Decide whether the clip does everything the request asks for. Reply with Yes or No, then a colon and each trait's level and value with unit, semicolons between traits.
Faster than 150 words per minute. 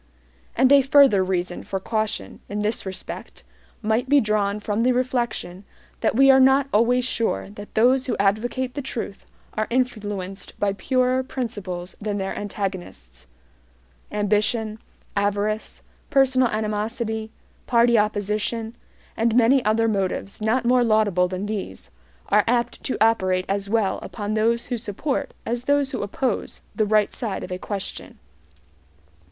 No: average, 145 wpm